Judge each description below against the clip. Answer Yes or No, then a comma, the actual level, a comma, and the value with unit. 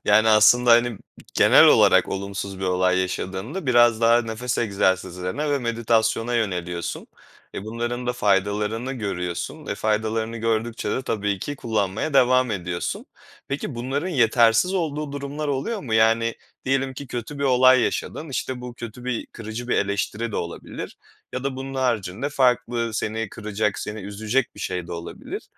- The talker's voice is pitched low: Yes, low, 115 Hz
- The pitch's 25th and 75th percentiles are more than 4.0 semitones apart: No, average, 3.7 semitones